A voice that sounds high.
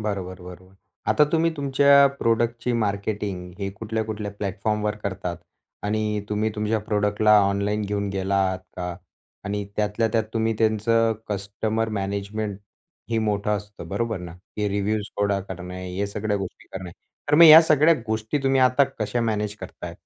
No: low, 105 Hz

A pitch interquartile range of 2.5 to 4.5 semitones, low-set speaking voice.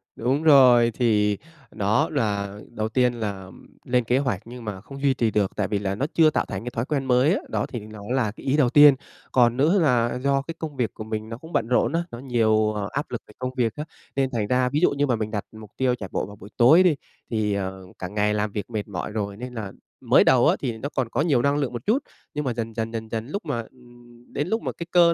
Yes: average, 4.2 semitones; low, 120 Hz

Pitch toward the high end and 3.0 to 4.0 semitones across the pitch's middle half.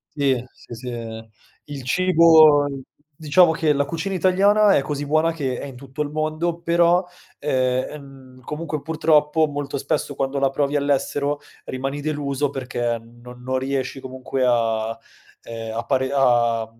No: medium, 140 Hz; average, 3.4 semitones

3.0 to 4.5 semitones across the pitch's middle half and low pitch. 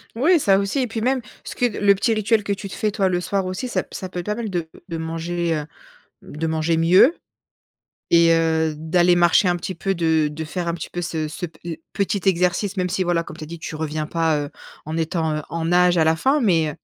No: average, 3.4 semitones; medium, 175 Hz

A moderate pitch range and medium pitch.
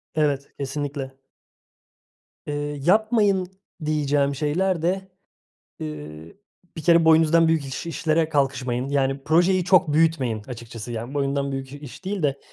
Yes: average, 3.5 semitones; medium, 145 Hz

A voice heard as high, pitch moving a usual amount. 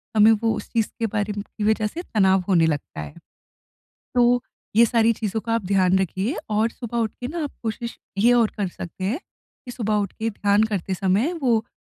Yes: high, 215 Hz; average, 3.0 semitones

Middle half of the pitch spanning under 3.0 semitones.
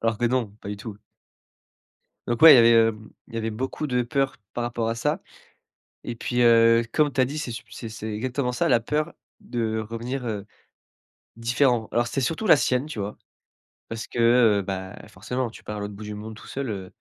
Yes: narrow, 2.5 semitones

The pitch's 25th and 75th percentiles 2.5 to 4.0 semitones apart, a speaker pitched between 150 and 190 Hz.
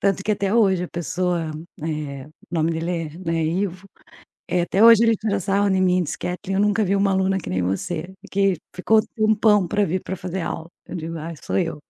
Yes: average, 3.2 semitones; medium, 185 Hz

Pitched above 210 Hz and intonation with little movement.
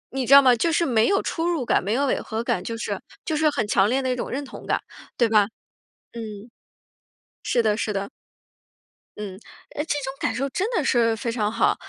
No: high, 240 Hz; average, 4.3 semitones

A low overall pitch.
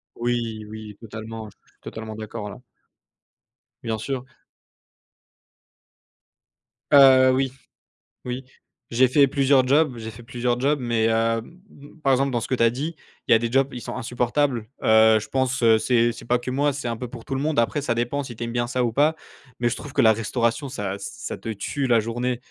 Yes: low, 120 Hz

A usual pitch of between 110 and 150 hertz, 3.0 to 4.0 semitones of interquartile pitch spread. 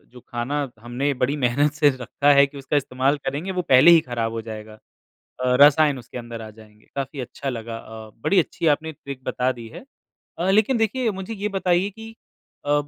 No: medium, 140 Hz; average, 5.1 semitones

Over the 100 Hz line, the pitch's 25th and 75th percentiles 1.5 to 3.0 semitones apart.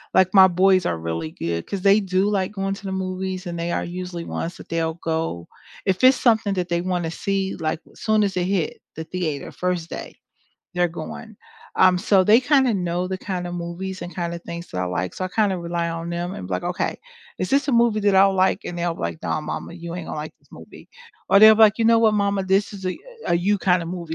Yes: medium, 185 Hz; narrow, 2.6 semitones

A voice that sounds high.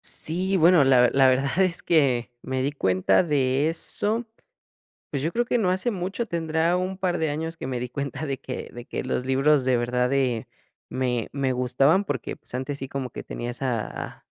No: medium, 140 Hz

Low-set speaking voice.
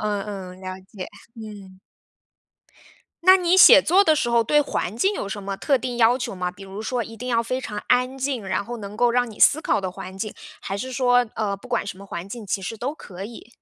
No: high, 225 Hz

